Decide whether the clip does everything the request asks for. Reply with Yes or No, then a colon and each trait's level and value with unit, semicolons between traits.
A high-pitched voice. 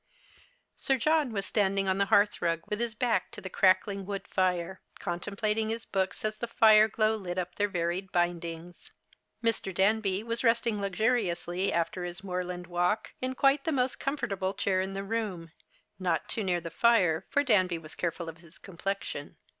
Yes: high, 195 Hz